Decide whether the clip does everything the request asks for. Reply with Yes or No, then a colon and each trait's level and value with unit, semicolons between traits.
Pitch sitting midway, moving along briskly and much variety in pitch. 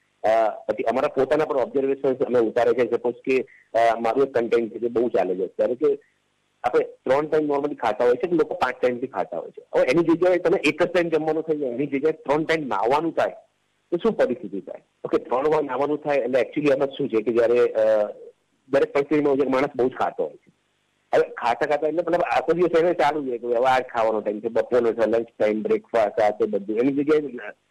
Yes: medium, 145 Hz; fast, 220 wpm; wide, 6.3 semitones